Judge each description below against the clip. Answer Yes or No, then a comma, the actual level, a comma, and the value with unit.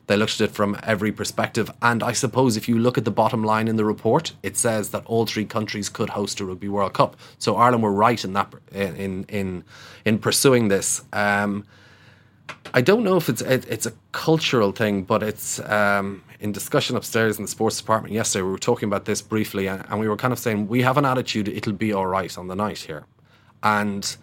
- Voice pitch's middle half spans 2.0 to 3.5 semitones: Yes, narrow, 2.6 semitones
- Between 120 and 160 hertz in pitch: No, low, 110 Hz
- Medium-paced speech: No, fast, 225 wpm